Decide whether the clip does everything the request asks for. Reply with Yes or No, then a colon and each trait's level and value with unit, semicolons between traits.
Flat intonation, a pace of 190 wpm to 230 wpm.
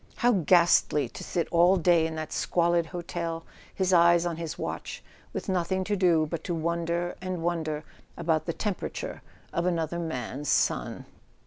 No: narrow, 1.5 semitones; average, 160 wpm